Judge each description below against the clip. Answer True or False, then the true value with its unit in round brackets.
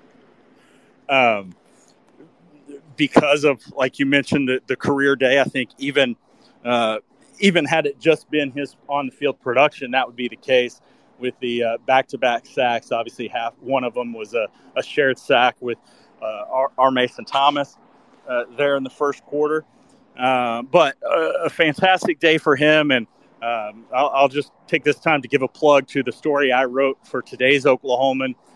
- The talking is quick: False (180 wpm)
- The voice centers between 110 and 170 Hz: True (140 Hz)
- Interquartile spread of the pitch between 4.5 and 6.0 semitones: False (2.9 semitones)